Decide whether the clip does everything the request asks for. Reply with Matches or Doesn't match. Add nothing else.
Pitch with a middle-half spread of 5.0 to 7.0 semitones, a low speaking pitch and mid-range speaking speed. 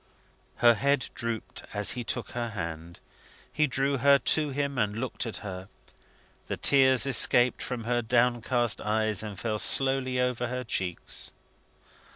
Doesn't match